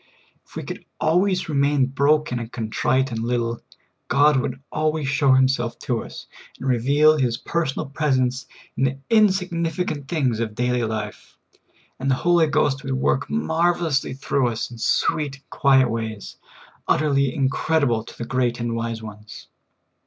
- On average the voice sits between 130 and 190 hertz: Yes, low, 135 Hz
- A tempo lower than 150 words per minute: No, average, 155 wpm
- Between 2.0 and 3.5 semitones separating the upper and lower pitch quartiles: No, average, 4.1 semitones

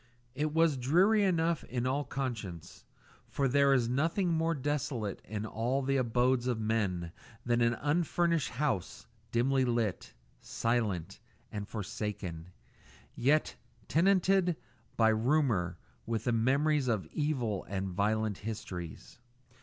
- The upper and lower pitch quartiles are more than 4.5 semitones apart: Yes, wide, 5.4 semitones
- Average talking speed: No, slow, 130 wpm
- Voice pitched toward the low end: Yes, low, 125 Hz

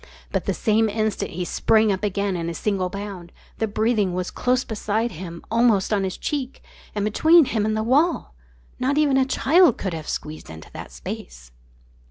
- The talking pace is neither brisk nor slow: Yes, average, 190 wpm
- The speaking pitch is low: No, high, 210 Hz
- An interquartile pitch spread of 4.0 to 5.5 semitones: Yes, average, 4.7 semitones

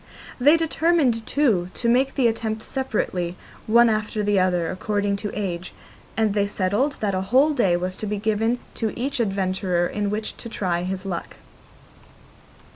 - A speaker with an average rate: Yes, average, 165 wpm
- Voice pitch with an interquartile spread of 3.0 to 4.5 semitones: Yes, average, 4.1 semitones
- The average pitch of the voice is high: Yes, high, 210 Hz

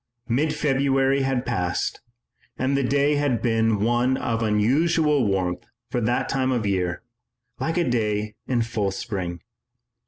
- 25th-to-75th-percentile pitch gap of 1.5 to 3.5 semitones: No, average, 4.4 semitones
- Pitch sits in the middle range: No, low, 120 Hz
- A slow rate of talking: No, average, 150 wpm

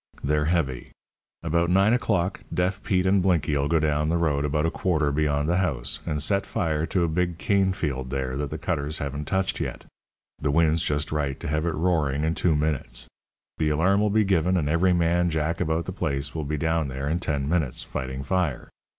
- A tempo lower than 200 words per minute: No, fast, 205 wpm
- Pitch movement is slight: No, average, 3.3 semitones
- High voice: No, very low, 80 Hz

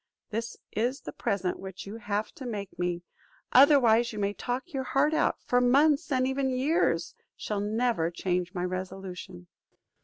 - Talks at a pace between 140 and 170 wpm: Yes, average, 160 wpm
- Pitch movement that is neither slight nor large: No, wide, 5.7 semitones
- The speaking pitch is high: Yes, high, 225 Hz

